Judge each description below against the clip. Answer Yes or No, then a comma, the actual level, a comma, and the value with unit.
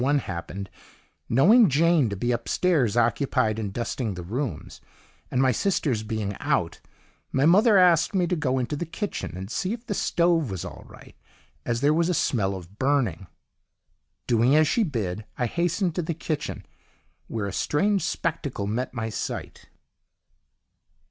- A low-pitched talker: Yes, low, 130 Hz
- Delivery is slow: No, average, 160 wpm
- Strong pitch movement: Yes, wide, 7.5 semitones